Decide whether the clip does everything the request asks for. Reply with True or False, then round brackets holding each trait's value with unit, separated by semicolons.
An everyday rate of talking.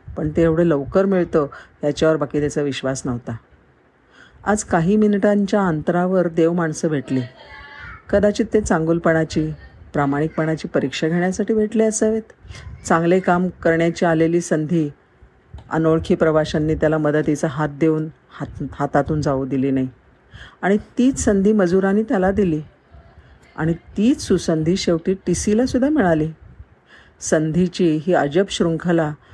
True (120 wpm)